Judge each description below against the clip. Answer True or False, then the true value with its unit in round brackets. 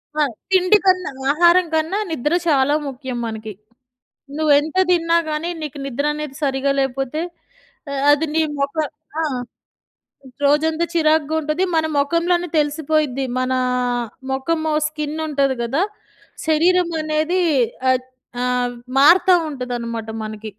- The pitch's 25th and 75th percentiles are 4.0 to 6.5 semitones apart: False (3.3 semitones)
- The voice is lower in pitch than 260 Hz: False (300 Hz)